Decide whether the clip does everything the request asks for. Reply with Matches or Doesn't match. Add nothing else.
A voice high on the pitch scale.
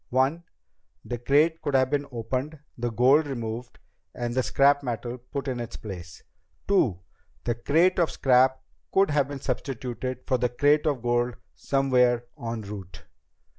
Doesn't match